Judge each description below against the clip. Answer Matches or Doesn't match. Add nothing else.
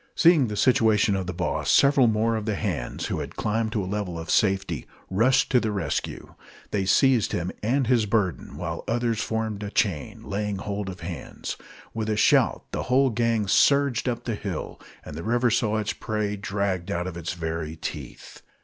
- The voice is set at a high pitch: Doesn't match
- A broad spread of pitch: Doesn't match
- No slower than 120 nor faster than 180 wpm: Doesn't match